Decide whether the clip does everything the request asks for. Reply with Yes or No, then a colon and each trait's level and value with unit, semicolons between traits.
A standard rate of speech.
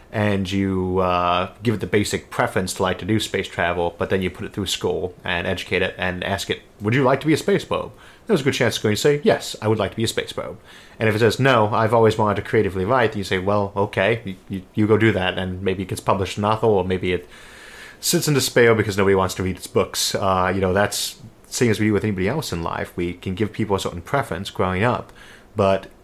No: fast, 270 wpm